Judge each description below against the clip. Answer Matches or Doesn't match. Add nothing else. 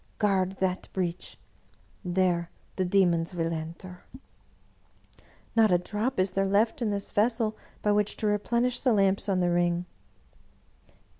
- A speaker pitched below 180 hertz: Doesn't match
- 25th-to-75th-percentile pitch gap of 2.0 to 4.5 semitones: Matches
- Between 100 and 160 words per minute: Matches